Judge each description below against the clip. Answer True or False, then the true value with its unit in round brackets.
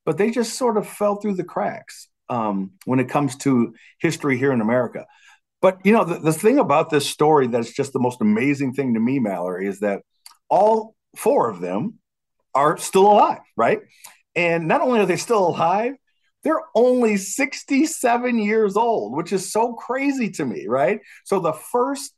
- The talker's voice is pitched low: False (200 Hz)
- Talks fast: False (185 wpm)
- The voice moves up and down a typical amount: False (8.8 semitones)